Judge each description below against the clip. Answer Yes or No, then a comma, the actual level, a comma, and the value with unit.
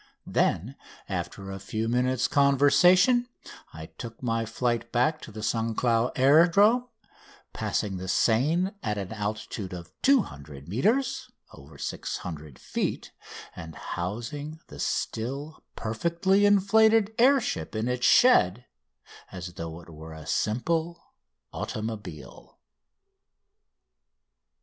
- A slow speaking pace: Yes, slow, 110 wpm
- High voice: No, low, 120 Hz